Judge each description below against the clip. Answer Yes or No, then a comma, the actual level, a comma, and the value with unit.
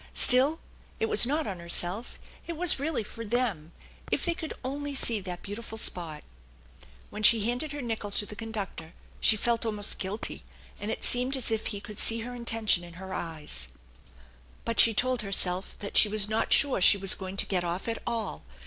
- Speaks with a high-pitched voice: Yes, high, 220 Hz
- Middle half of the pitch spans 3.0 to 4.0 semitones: No, average, 4.4 semitones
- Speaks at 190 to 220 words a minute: Yes, average, 195 wpm